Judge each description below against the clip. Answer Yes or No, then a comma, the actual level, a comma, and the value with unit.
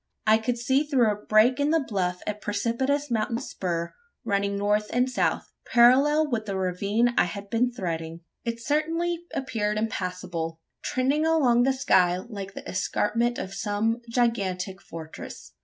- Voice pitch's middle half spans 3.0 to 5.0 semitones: Yes, average, 4.6 semitones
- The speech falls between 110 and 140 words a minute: No, average, 155 wpm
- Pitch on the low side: No, high, 220 Hz